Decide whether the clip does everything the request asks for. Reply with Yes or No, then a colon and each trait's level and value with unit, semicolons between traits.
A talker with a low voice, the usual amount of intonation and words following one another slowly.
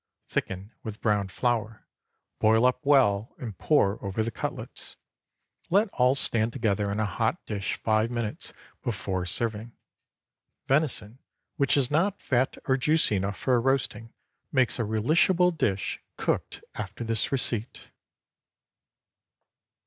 Yes: low, 115 Hz; average, 4.2 semitones; slow, 125 wpm